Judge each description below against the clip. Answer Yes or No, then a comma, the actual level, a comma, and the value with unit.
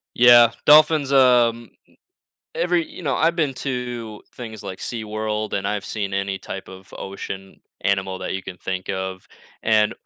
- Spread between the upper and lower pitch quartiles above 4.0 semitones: Yes, average, 4.4 semitones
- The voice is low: Yes, low, 110 Hz